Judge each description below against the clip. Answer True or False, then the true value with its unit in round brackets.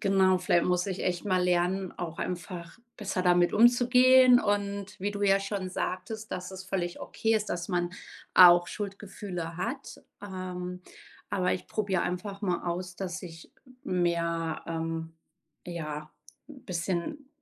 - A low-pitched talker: False (185 Hz)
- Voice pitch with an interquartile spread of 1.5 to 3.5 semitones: True (2.5 semitones)